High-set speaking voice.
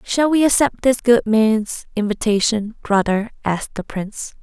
Yes: high, 225 Hz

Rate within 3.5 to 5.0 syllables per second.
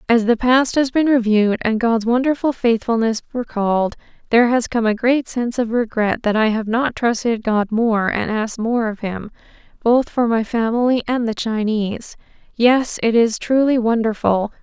Yes: 4.9 syllables/s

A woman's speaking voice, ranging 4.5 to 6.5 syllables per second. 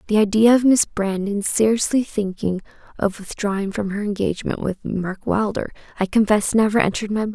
Yes: female; 5.5 syllables/s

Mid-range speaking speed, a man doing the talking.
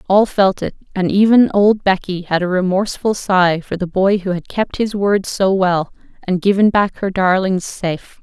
No: average, 195 wpm; female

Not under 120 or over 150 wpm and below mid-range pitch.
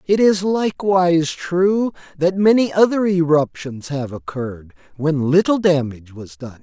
No: slow, 135 wpm; medium, 165 Hz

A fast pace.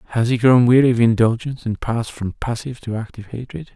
Yes: fast, 210 wpm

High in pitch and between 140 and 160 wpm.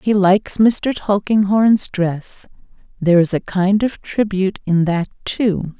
Yes: high, 195 Hz; average, 145 wpm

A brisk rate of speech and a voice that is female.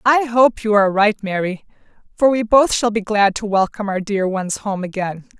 Yes: fast, 210 wpm; female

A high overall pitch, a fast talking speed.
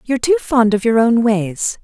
Yes: high, 230 Hz; fast, 230 wpm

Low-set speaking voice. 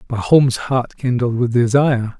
Yes: low, 125 Hz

